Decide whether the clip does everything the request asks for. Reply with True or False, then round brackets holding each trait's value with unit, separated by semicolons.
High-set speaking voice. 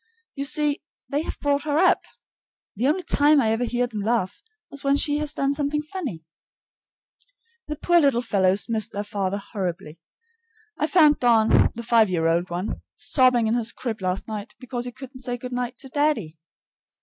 True (245 Hz)